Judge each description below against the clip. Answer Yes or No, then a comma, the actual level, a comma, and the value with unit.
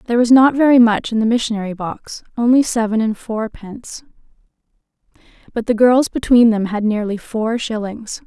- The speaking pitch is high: Yes, high, 225 Hz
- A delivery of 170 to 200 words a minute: No, average, 160 wpm